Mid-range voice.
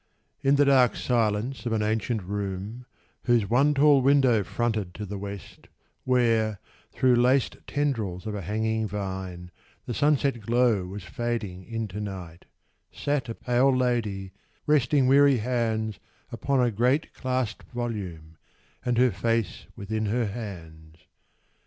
No: low, 115 Hz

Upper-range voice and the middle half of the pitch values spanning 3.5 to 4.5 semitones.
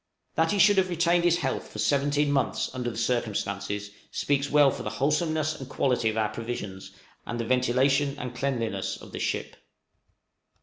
No: low, 135 Hz; average, 4.2 semitones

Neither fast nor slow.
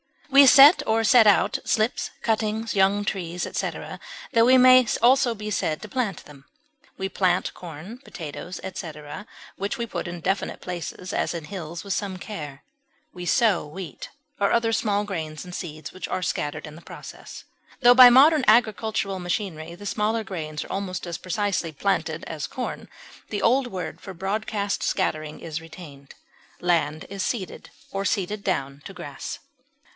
Yes: average, 165 wpm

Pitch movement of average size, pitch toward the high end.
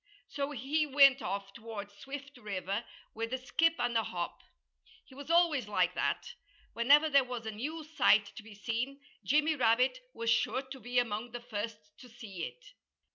Yes: average, 4.2 semitones; high, 245 Hz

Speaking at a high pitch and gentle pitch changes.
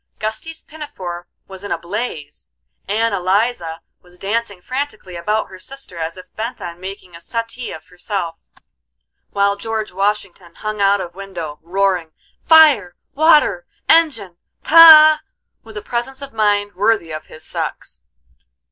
No: high, 200 Hz; average, 4.8 semitones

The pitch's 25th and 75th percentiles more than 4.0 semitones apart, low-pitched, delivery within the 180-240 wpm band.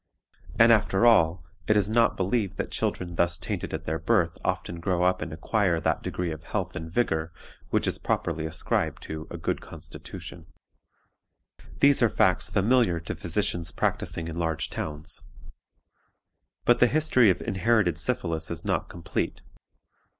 No: average, 4.8 semitones; very low, 90 Hz; average, 155 wpm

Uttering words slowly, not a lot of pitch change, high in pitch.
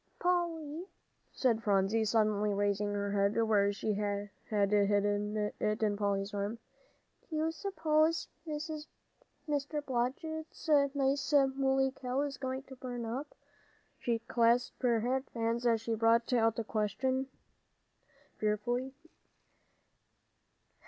No: slow, 115 wpm; average, 4.6 semitones; high, 235 Hz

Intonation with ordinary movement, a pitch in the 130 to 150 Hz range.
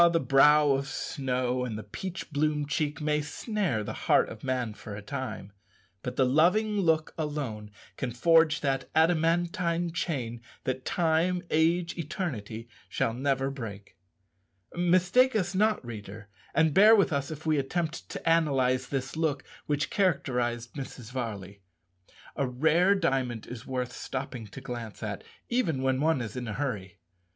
Yes: average, 5.0 semitones; medium, 140 Hz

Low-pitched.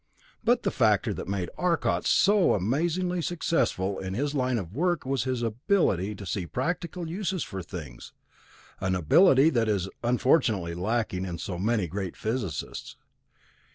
Yes: low, 115 Hz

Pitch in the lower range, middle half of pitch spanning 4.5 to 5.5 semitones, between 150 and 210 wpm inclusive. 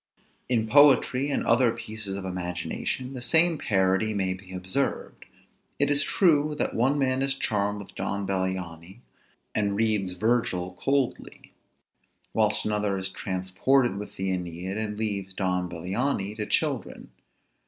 No: low, 105 Hz; average, 5.2 semitones; average, 140 wpm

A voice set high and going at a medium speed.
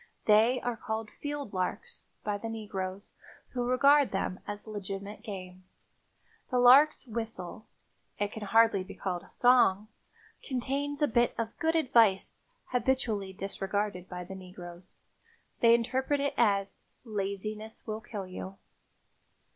No: high, 215 Hz; slow, 125 wpm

